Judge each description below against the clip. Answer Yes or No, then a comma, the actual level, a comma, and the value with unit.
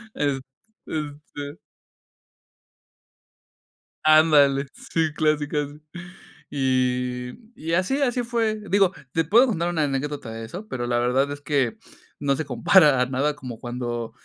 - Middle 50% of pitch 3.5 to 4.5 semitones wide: Yes, average, 4.1 semitones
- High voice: No, medium, 145 Hz